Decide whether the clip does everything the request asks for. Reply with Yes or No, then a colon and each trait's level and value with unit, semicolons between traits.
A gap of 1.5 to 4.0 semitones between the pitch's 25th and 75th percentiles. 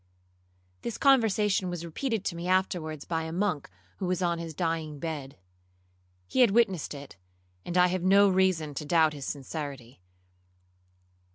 Yes: average, 3.5 semitones